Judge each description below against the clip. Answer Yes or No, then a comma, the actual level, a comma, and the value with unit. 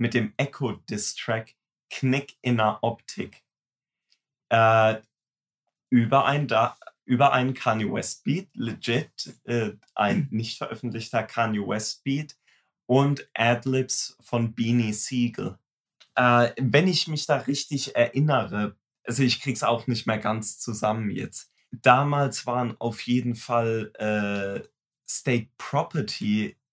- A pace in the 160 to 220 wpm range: No, slow, 125 wpm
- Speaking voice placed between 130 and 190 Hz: No, low, 120 Hz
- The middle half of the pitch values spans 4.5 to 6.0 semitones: No, average, 3.2 semitones